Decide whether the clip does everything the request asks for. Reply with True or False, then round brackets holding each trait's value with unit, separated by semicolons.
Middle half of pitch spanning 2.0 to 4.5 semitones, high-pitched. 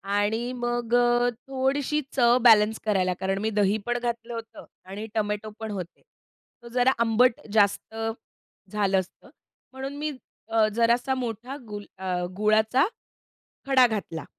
True (2.8 semitones; 225 Hz)